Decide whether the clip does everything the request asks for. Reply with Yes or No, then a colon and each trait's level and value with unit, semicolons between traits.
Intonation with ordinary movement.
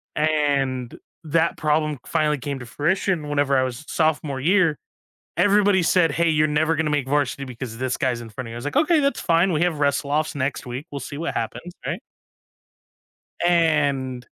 Yes: average, 3.5 semitones